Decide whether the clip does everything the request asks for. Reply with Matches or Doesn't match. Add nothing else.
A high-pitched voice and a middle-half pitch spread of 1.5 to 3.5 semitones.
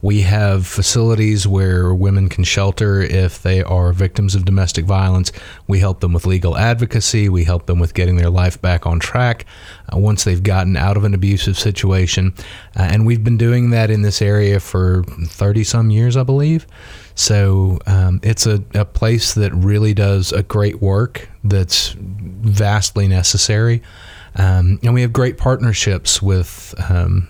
Doesn't match